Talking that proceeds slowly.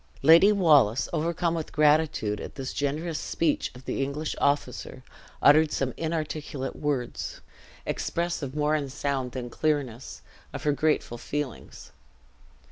Yes: slow, 125 wpm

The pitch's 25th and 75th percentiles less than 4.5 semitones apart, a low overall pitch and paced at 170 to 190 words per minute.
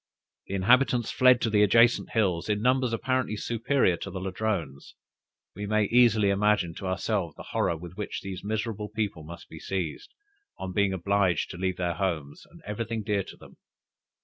Yes: average, 3.3 semitones; low, 100 Hz; average, 175 wpm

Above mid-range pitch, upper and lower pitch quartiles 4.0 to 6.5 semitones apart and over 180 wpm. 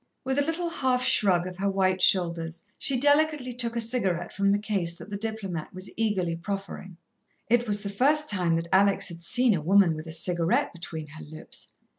Yes: high, 195 Hz; wide, 5.6 semitones; average, 200 wpm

